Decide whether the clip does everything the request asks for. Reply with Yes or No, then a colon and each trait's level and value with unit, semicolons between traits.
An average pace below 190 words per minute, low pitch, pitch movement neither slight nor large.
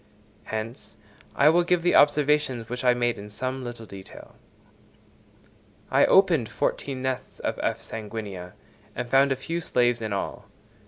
Yes: average, 150 wpm; low, 125 Hz; average, 4.5 semitones